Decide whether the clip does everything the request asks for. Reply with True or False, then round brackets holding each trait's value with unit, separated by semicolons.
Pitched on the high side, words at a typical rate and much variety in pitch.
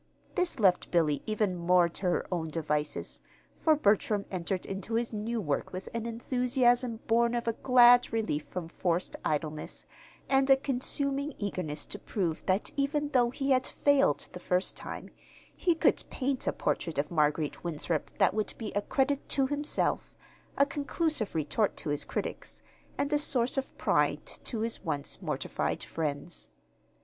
True (220 Hz; 160 wpm; 7.5 semitones)